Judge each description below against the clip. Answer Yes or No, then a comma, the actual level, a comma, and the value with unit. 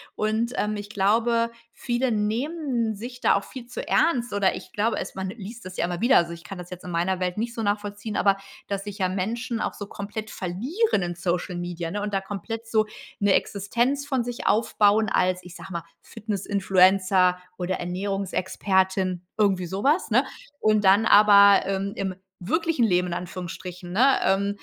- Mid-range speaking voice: No, high, 200 Hz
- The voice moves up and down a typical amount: Yes, average, 3.4 semitones